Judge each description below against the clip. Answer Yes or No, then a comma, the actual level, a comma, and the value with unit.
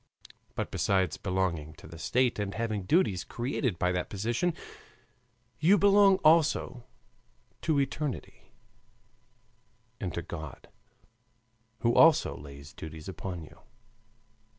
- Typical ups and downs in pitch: No, wide, 8.7 semitones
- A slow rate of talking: Yes, slow, 110 wpm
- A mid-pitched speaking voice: No, low, 100 Hz